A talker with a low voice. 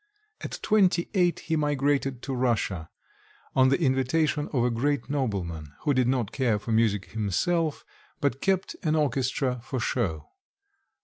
Yes: low, 130 Hz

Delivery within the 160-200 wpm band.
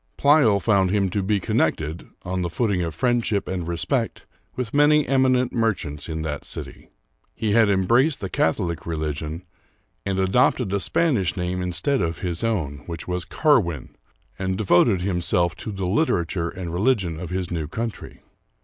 Yes: average, 165 wpm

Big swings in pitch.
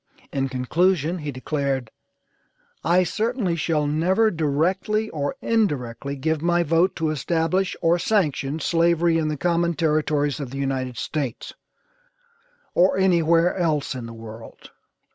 No: average, 3.9 semitones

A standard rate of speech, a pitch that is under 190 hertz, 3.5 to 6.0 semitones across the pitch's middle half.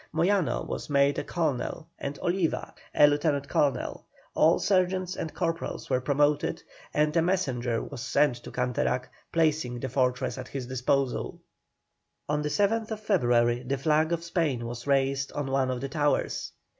Yes: average, 155 wpm; medium, 140 Hz; average, 4.3 semitones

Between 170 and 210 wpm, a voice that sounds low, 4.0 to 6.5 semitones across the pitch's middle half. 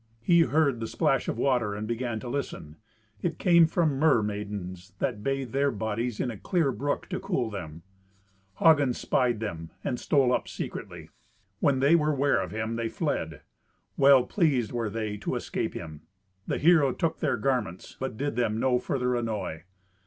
Yes: average, 175 wpm; low, 125 Hz; average, 4.8 semitones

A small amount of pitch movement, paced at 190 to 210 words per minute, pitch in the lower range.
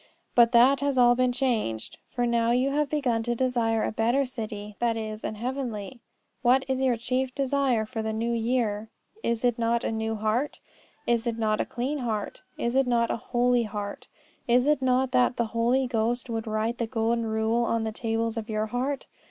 No: narrow, 2.2 semitones; average, 200 wpm; high, 235 Hz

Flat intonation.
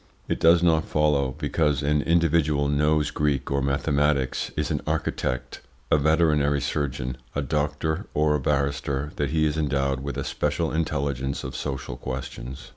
Yes: narrow, 1.8 semitones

